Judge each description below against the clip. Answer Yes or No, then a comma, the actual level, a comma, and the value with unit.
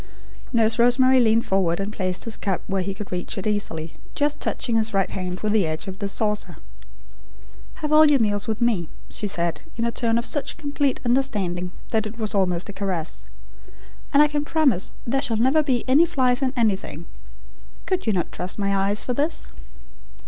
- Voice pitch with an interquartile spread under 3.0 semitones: No, average, 5.0 semitones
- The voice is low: No, high, 220 Hz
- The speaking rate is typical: Yes, average, 195 wpm